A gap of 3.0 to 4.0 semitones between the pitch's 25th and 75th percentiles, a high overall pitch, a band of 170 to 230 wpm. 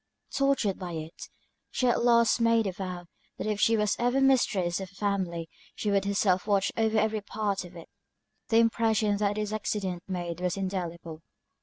Yes: average, 3.4 semitones; high, 200 Hz; average, 180 wpm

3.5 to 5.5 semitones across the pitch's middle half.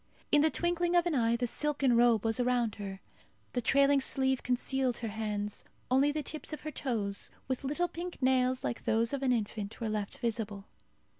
Yes: average, 4.0 semitones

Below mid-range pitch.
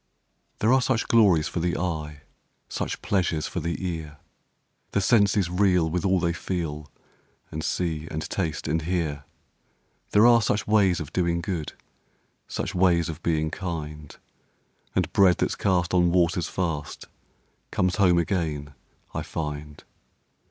Yes: very low, 85 Hz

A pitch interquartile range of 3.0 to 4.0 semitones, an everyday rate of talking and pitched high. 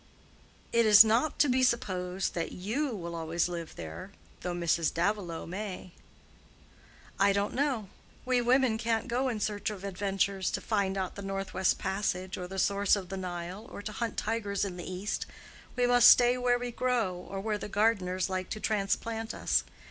Yes: average, 3.7 semitones; average, 180 wpm; high, 200 Hz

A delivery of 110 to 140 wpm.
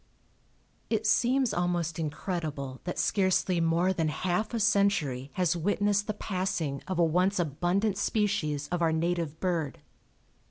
Yes: slow, 135 wpm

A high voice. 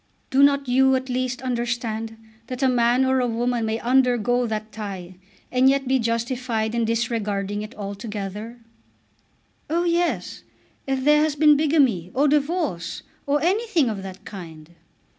Yes: high, 245 Hz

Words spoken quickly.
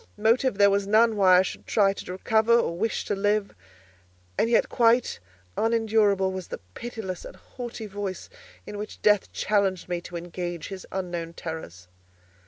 No: average, 165 wpm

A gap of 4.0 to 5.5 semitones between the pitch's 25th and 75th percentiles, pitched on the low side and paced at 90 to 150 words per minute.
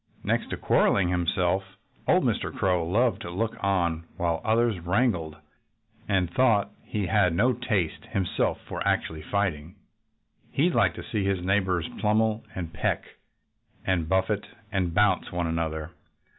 No: average, 3.5 semitones; very low, 95 Hz; average, 145 wpm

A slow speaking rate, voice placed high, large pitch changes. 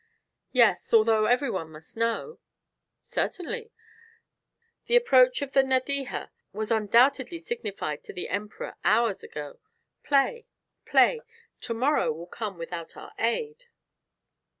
Yes: slow, 120 wpm; high, 240 Hz; wide, 8.0 semitones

